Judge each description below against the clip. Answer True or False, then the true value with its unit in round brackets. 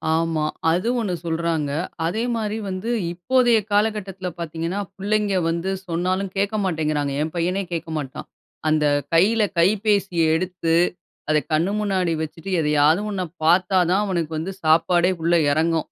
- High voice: False (175 Hz)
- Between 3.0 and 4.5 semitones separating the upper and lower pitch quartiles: True (3.4 semitones)